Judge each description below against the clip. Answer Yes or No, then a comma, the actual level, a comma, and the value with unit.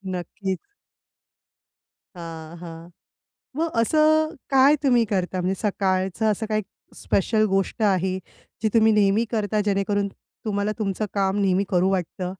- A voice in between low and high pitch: No, high, 200 Hz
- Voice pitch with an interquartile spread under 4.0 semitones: Yes, average, 2.8 semitones